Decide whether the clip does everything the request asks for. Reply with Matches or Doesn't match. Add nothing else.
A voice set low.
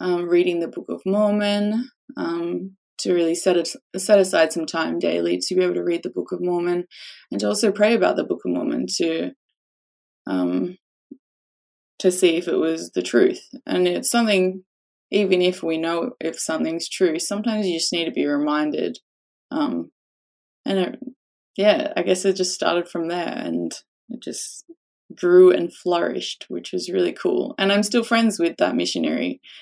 Doesn't match